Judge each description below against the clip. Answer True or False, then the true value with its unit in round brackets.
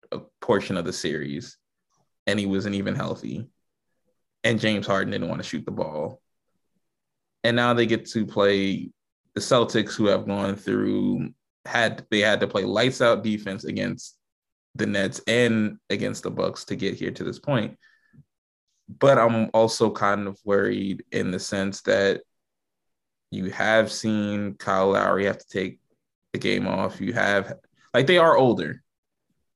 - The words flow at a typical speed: True (160 wpm)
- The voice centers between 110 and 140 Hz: False (100 Hz)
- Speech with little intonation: True (2.3 semitones)